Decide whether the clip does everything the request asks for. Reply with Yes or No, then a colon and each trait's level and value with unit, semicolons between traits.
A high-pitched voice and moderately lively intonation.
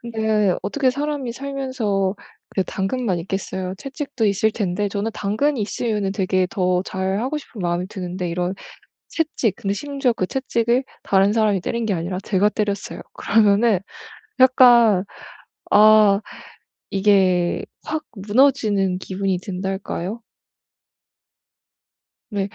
Yes: high, 205 Hz; average, 3.8 semitones